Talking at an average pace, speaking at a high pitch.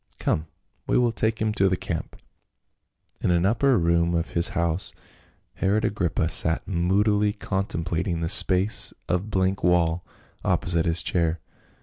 No: average, 145 wpm; very low, 90 Hz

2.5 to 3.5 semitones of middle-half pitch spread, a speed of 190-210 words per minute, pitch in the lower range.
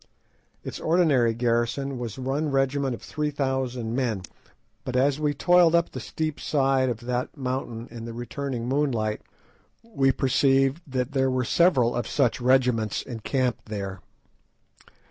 No: average, 2.8 semitones; average, 145 wpm; low, 130 Hz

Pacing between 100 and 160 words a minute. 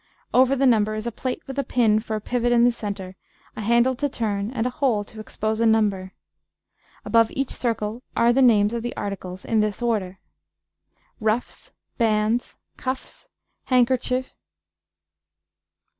Yes: average, 155 wpm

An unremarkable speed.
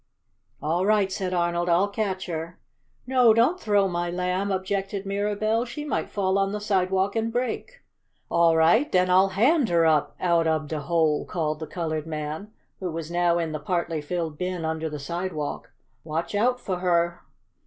Yes: average, 175 wpm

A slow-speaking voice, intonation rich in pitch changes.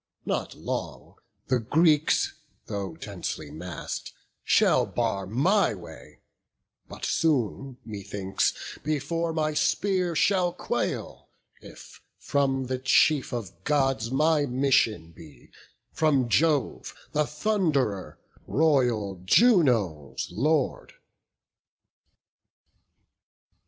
Yes: slow, 90 wpm; wide, 6.6 semitones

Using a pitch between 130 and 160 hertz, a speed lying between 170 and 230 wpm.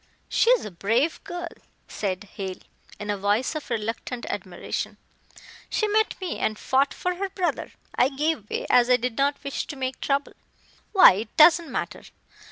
No: very high, 260 Hz; average, 175 wpm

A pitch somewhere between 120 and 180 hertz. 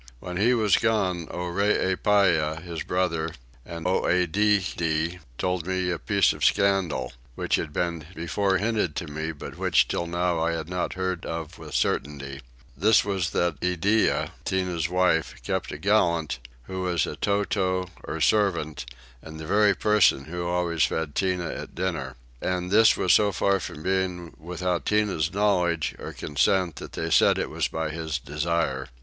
No: very low, 90 Hz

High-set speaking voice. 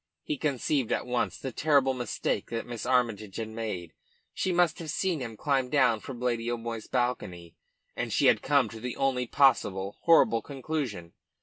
No: low, 125 Hz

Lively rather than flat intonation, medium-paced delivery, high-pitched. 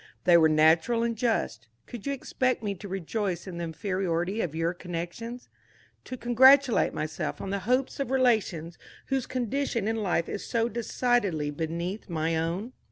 Yes: wide, 6.1 semitones; average, 165 wpm; high, 200 Hz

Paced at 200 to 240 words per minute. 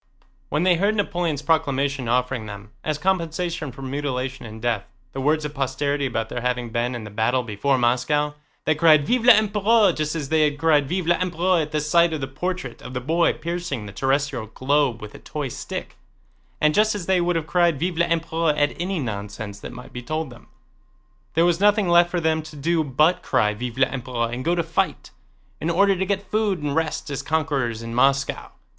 Yes: fast, 205 wpm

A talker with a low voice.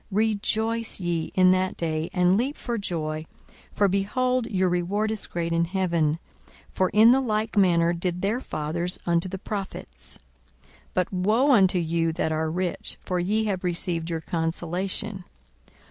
No: medium, 185 Hz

